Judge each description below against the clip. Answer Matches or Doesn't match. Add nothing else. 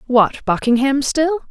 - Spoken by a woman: Matches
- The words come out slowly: Matches